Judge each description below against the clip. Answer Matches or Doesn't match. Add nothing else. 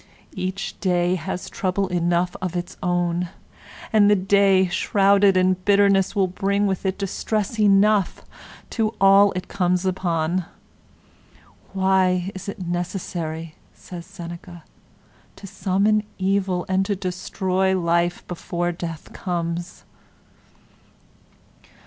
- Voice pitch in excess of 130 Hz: Matches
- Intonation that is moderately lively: Doesn't match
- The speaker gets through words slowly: Matches